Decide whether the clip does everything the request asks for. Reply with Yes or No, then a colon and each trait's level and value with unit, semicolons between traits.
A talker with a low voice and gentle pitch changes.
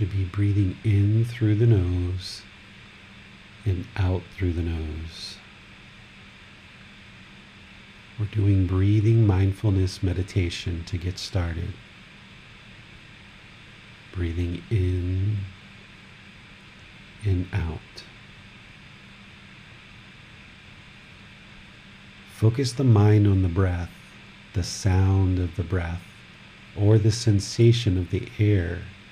Yes: low, 100 Hz; narrow, 2.1 semitones